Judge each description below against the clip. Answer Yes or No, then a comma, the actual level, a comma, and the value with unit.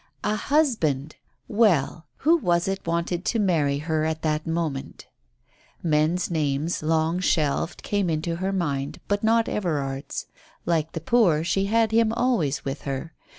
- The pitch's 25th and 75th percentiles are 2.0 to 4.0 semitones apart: No, average, 4.9 semitones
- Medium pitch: Yes, medium, 165 Hz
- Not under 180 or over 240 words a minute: No, average, 150 wpm